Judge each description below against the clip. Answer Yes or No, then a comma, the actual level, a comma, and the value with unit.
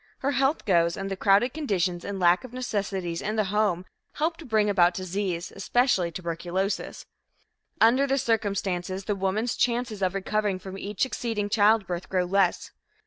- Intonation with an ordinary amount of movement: Yes, average, 3.4 semitones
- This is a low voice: No, high, 200 Hz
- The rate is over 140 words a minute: Yes, average, 160 wpm